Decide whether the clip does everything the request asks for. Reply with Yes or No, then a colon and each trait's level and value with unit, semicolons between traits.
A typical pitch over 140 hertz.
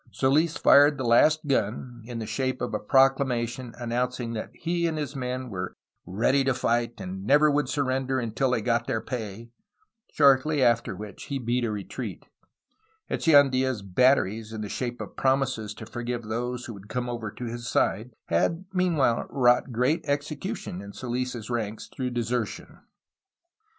No: low, 125 Hz